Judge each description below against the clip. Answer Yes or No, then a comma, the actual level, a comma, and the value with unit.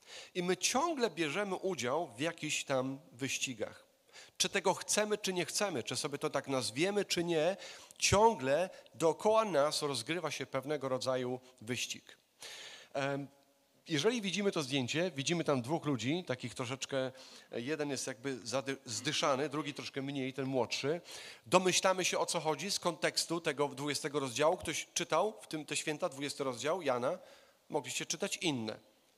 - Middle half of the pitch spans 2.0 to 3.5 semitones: No, average, 5.0 semitones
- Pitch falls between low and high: Yes, medium, 150 Hz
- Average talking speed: Yes, average, 145 wpm